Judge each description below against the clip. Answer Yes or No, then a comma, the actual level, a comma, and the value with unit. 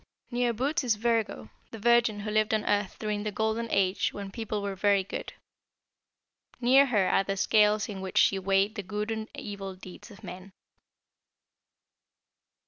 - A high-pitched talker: Yes, high, 210 Hz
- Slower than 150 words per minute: No, average, 165 wpm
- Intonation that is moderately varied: No, narrow, 2.3 semitones